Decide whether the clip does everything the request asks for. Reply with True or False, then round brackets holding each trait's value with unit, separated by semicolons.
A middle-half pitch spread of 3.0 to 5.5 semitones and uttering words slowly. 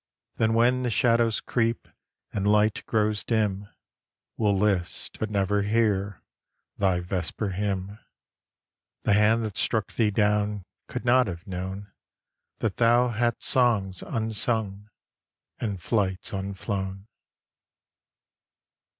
False (2.5 semitones; 110 wpm)